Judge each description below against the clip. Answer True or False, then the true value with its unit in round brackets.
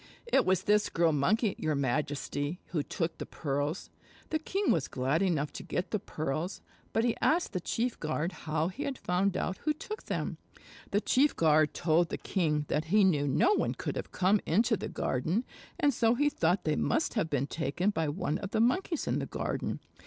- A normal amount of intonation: False (6.7 semitones)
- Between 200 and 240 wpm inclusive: True (205 wpm)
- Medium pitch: True (175 Hz)